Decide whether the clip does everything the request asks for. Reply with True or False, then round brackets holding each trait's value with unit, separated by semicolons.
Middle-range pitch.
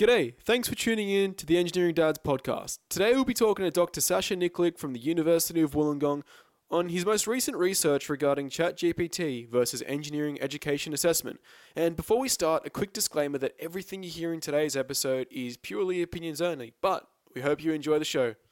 True (165 Hz)